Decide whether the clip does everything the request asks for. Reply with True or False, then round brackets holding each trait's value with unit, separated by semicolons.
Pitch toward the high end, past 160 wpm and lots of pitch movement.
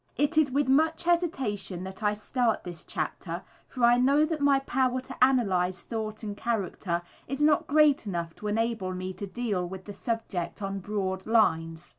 True (220 Hz; 180 wpm; 6.0 semitones)